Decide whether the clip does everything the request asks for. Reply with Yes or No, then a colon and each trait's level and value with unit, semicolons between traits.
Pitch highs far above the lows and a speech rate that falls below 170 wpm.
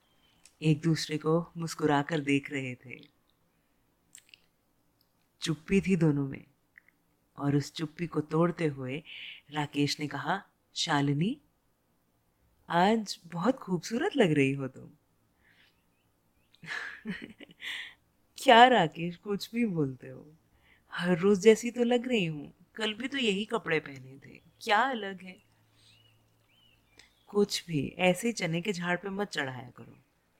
Yes: wide, 6.4 semitones; average, 125 wpm